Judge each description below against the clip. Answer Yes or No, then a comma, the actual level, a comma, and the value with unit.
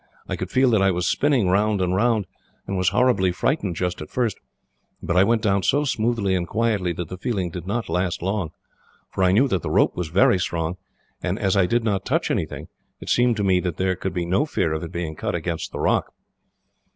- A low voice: Yes, very low, 95 Hz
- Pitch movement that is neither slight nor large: Yes, average, 3.7 semitones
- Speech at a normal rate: No, fast, 230 wpm